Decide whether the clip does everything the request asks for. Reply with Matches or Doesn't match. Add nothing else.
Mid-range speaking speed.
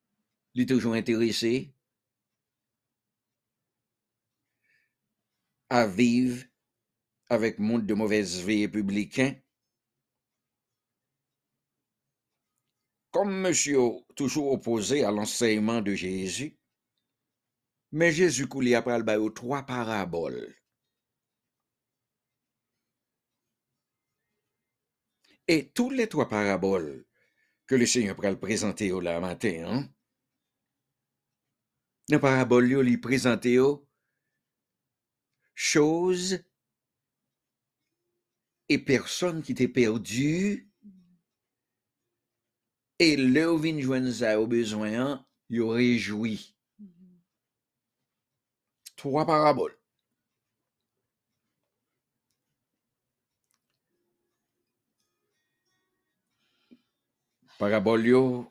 Doesn't match